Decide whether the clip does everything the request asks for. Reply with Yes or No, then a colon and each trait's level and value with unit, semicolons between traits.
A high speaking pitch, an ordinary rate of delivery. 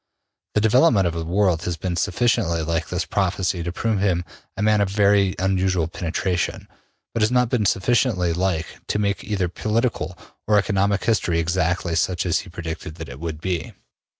No: very low, 95 Hz; average, 180 wpm